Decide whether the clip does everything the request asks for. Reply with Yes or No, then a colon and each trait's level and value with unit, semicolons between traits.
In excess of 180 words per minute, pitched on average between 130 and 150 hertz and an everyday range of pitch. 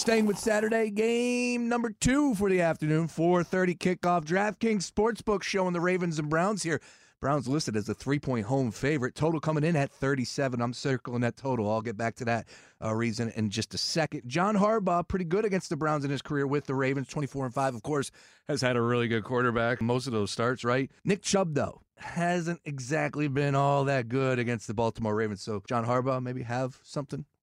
No: average, 200 wpm; medium, 140 Hz; wide, 6.2 semitones